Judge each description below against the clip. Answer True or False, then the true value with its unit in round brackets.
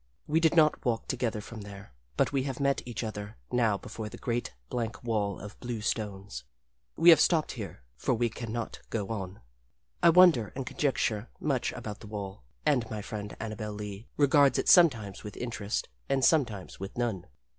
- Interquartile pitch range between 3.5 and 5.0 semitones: True (4.2 semitones)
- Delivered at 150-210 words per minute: True (185 wpm)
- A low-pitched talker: True (115 Hz)